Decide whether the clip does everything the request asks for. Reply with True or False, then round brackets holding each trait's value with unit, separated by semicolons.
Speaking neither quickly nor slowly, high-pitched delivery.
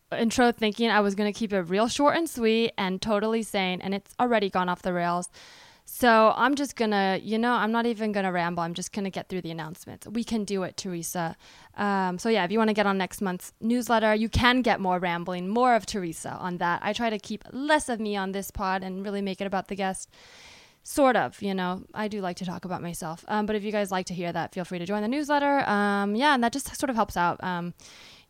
False (260 wpm; 205 Hz)